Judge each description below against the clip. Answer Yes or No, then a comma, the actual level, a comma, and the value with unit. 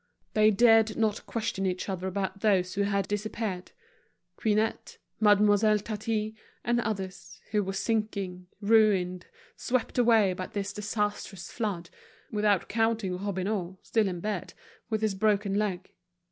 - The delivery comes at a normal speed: No, slow, 130 wpm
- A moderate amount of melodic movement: No, narrow, 2.3 semitones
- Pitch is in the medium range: No, high, 205 Hz